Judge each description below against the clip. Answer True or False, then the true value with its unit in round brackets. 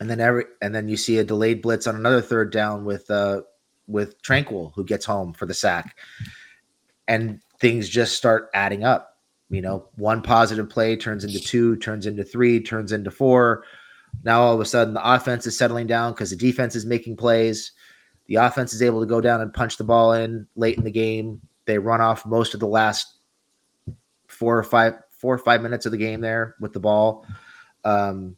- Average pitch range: False (1.5 semitones)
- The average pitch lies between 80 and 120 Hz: True (115 Hz)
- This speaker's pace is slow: False (205 wpm)